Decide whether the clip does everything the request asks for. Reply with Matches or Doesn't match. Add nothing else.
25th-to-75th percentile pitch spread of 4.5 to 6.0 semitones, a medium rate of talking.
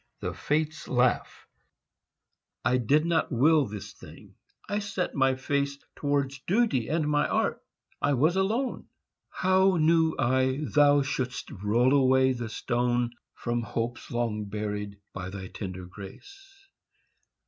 Doesn't match